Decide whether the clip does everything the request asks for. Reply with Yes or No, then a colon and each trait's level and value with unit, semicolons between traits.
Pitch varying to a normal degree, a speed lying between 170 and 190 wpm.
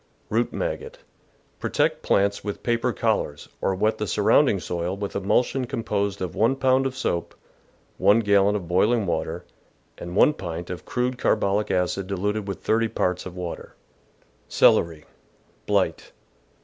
No: average, 4.2 semitones; average, 160 wpm